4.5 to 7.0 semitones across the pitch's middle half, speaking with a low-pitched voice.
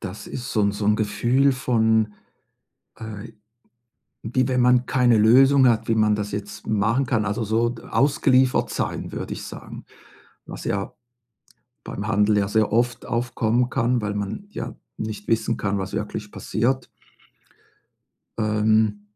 No: average, 2.7 semitones; low, 110 Hz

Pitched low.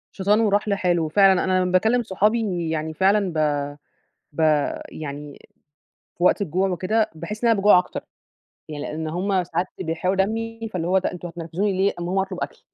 No: medium, 185 Hz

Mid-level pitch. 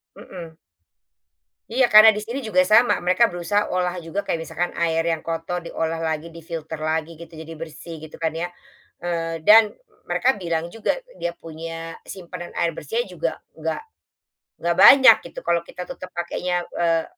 Yes: medium, 170 Hz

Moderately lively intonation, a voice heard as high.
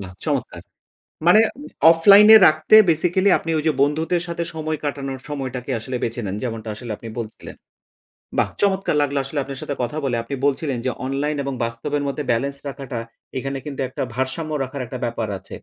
No: average, 3.5 semitones; medium, 140 Hz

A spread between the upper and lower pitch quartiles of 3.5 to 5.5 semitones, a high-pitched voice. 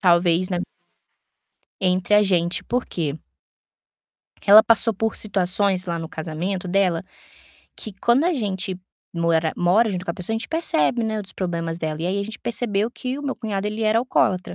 Yes: average, 4.1 semitones; high, 195 Hz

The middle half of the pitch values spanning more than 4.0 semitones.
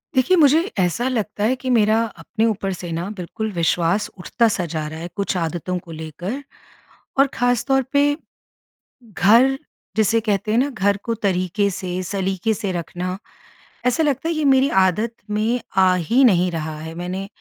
Yes: average, 5.2 semitones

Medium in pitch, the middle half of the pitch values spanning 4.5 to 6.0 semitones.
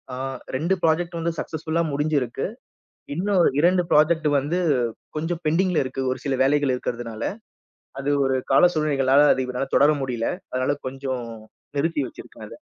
No: medium, 145 Hz; average, 3.8 semitones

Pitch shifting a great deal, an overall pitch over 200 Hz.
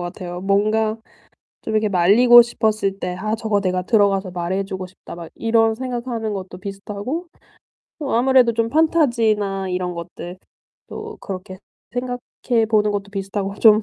No: average, 3.3 semitones; high, 210 Hz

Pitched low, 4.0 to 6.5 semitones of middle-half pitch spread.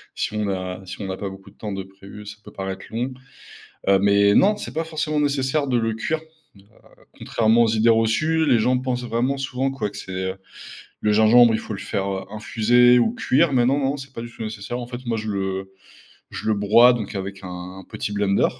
Yes: low, 110 Hz; average, 4.4 semitones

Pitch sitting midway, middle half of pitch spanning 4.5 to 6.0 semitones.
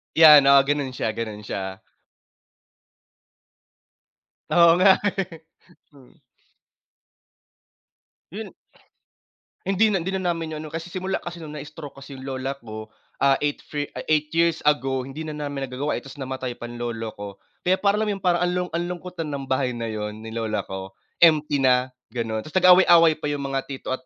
Yes: medium, 145 Hz; average, 4.9 semitones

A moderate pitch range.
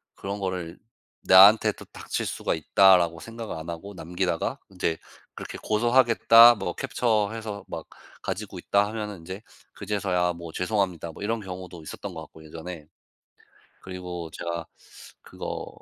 Yes: average, 3.6 semitones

